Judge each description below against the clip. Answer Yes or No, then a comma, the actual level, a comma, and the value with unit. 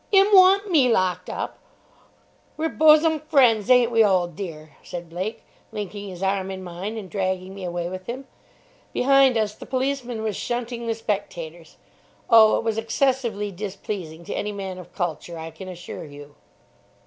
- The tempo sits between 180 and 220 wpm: No, average, 165 wpm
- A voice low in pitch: No, high, 205 Hz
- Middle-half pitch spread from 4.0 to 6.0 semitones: Yes, average, 5.2 semitones